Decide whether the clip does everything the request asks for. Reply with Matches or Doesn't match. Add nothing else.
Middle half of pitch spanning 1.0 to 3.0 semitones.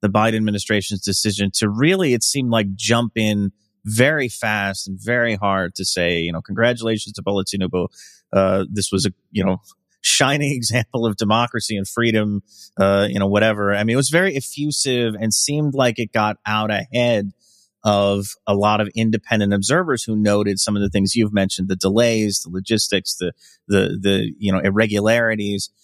Matches